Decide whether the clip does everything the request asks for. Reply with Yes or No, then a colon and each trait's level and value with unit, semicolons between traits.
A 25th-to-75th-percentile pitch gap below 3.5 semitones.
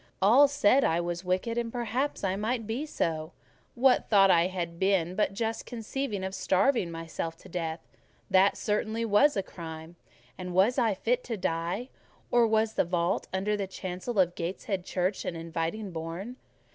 No: average, 4.8 semitones